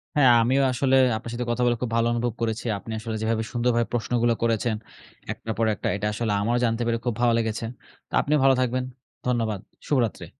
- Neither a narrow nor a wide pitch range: No, narrow, 1.5 semitones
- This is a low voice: Yes, low, 115 Hz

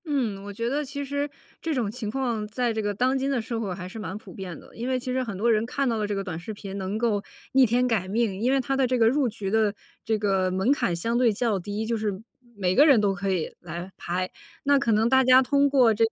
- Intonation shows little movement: No, average, 4.2 semitones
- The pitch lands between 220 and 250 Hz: Yes, high, 225 Hz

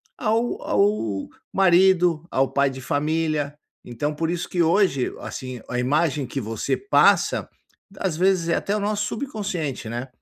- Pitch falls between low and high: Yes, medium, 160 Hz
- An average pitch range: No, wide, 6.1 semitones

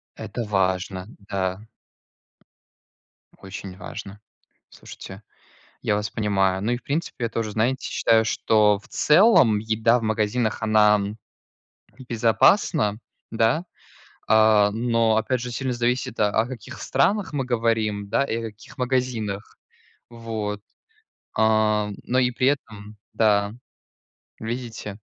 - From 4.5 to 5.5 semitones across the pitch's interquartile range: No, average, 2.7 semitones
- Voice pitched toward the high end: No, low, 110 Hz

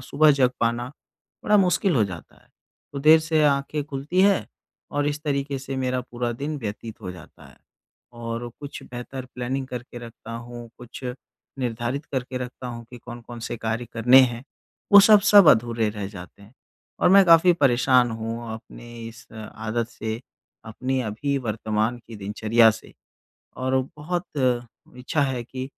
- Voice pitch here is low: Yes, low, 125 Hz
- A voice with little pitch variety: No, average, 3.3 semitones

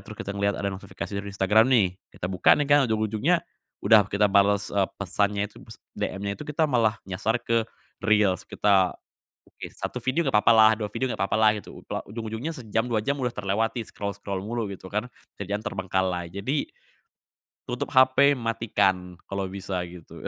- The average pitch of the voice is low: Yes, low, 105 Hz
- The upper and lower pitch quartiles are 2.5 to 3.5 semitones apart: Yes, average, 2.8 semitones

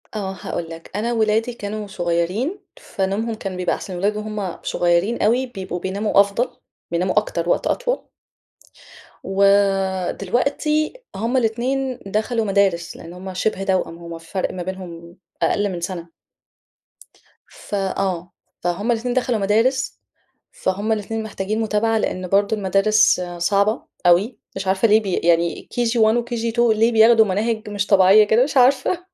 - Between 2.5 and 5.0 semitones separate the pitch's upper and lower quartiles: Yes, average, 3.3 semitones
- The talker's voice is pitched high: Yes, high, 205 Hz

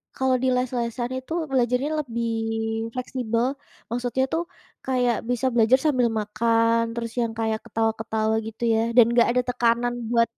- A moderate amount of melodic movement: No, narrow, 1.7 semitones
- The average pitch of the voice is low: No, high, 235 Hz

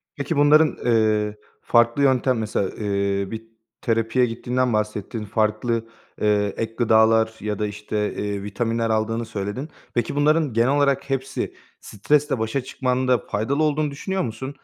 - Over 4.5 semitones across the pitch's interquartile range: No, average, 3.9 semitones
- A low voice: Yes, low, 115 Hz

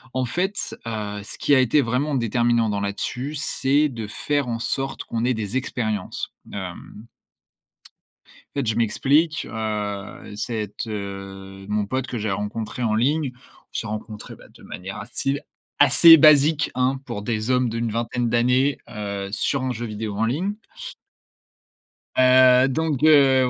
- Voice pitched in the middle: No, low, 120 Hz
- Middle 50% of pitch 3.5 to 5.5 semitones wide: Yes, average, 4.1 semitones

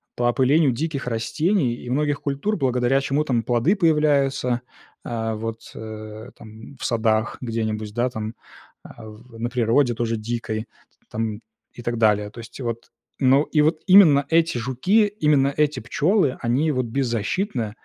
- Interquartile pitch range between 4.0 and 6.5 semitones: Yes, average, 4.3 semitones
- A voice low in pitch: Yes, low, 125 Hz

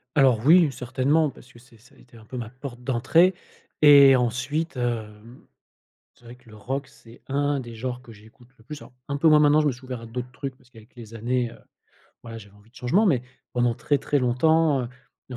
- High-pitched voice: No, low, 125 Hz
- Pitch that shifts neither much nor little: Yes, average, 3.2 semitones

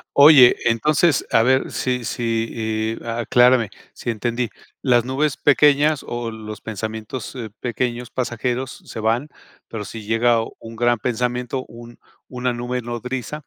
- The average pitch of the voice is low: Yes, low, 120 Hz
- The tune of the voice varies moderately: No, narrow, 2.1 semitones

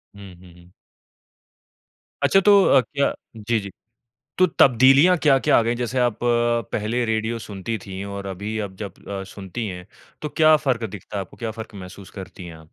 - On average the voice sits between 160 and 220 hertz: No, low, 110 Hz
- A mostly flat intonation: No, average, 4.1 semitones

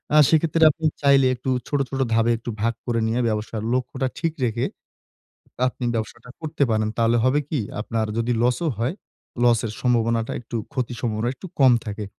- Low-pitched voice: Yes, low, 120 Hz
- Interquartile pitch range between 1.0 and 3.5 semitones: Yes, average, 2.8 semitones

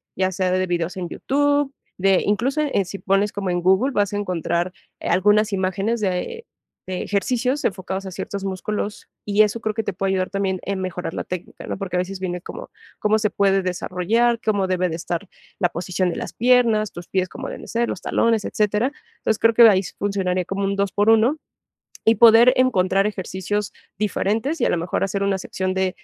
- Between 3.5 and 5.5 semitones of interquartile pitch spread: No, average, 2.9 semitones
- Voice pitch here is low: No, high, 195 Hz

